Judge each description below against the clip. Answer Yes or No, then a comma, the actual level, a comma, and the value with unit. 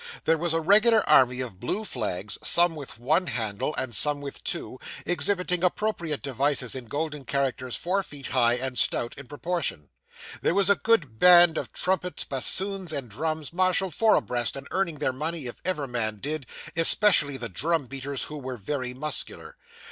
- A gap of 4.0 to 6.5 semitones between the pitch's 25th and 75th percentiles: Yes, wide, 5.5 semitones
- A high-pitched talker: No, medium, 145 Hz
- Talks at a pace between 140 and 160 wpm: No, average, 175 wpm